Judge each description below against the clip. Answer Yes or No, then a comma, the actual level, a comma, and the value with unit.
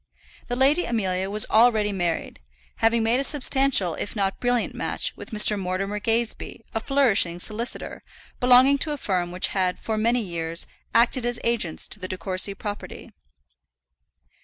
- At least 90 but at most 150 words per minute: No, average, 160 wpm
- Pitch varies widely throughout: No, average, 4.5 semitones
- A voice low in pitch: No, high, 215 Hz